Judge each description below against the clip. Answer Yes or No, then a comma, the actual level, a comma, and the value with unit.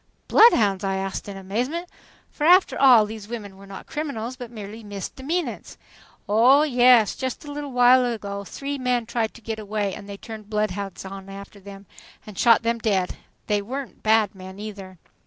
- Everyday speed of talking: Yes, average, 175 wpm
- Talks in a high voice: Yes, high, 220 Hz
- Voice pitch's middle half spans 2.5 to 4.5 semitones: Yes, average, 3.9 semitones